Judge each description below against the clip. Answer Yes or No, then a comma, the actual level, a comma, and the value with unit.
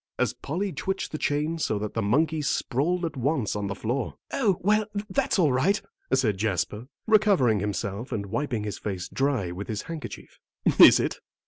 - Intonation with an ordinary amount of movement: No, wide, 7.8 semitones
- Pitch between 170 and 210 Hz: No, low, 130 Hz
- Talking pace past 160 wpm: Yes, average, 180 wpm